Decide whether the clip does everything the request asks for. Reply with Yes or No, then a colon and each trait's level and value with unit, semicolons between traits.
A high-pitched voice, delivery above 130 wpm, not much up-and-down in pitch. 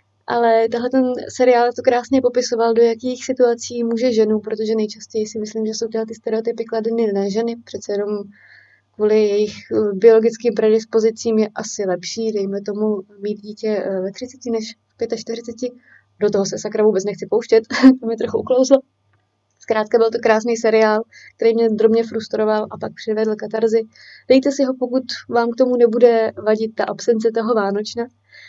Yes: high, 225 Hz; average, 165 wpm; narrow, 1.8 semitones